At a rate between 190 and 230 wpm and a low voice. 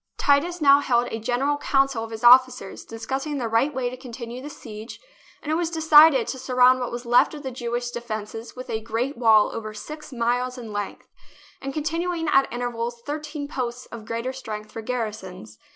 No: average, 195 wpm; high, 245 Hz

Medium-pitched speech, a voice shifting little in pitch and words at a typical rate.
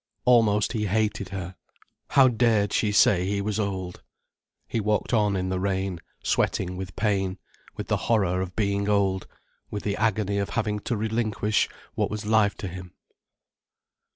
No: low, 100 Hz; narrow, 2.1 semitones; average, 160 wpm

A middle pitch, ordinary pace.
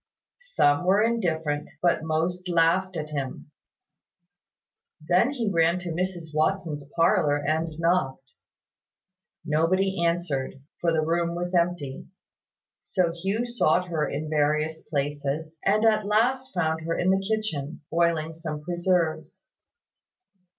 No: medium, 170 Hz; slow, 120 wpm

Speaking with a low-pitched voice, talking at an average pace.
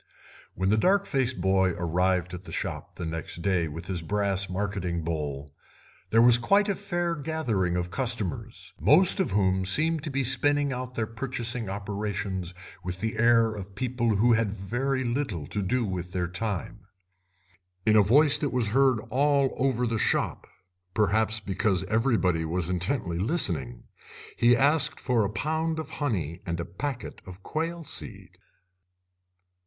Yes: low, 110 Hz; average, 160 wpm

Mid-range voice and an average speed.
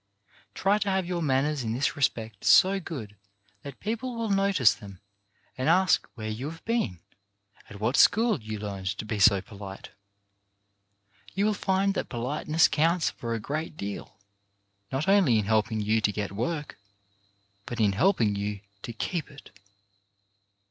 No: low, 130 Hz; average, 160 wpm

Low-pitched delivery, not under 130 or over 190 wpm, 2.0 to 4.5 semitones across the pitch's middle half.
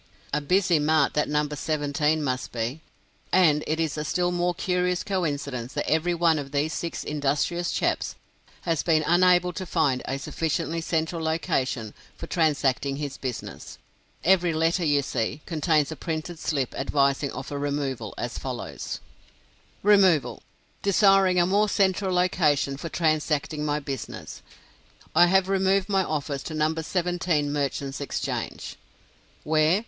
No: medium, 155 Hz; average, 145 wpm; average, 3.6 semitones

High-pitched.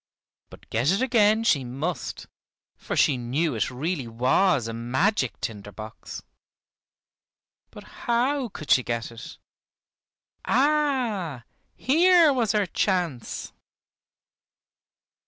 No: medium, 170 Hz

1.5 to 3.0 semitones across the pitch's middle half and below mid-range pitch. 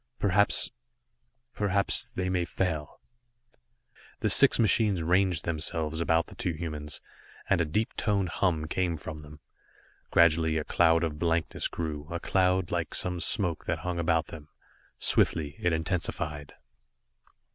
Yes: narrow, 2.6 semitones; very low, 85 Hz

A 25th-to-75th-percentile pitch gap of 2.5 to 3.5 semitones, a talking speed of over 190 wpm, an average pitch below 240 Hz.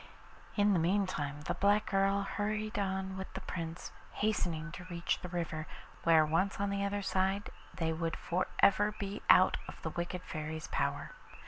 No: average, 3.2 semitones; average, 175 wpm; medium, 185 Hz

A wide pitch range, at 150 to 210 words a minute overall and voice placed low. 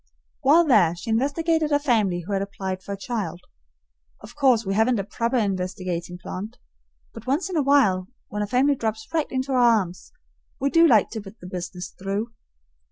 No: wide, 5.7 semitones; average, 190 wpm; high, 220 Hz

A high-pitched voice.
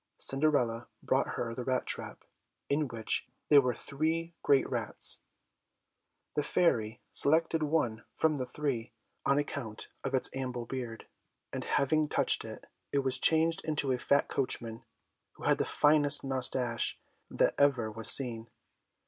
No: low, 135 Hz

